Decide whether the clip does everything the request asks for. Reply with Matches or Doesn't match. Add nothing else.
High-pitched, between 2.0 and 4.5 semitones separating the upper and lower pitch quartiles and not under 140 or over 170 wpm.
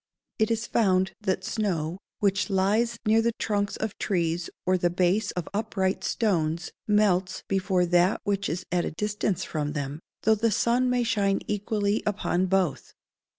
Matches